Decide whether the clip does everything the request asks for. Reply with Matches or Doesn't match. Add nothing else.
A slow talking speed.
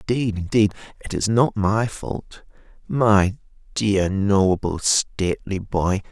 Matches